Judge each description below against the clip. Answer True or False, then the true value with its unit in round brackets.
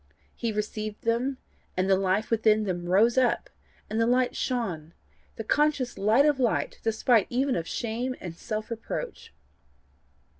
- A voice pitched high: True (225 Hz)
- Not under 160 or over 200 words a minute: False (150 wpm)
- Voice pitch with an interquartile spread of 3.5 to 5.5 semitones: False (3.1 semitones)